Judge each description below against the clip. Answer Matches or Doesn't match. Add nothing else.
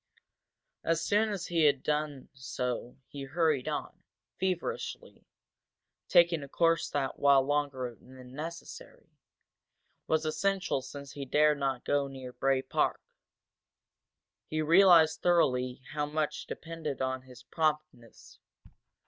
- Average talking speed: Doesn't match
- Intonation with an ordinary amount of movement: Matches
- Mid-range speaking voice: Matches